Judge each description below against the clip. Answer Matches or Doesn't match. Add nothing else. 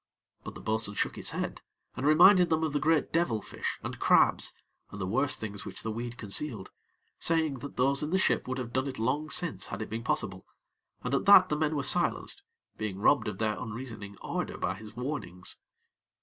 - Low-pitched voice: Matches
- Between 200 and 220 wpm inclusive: Matches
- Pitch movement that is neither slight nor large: Doesn't match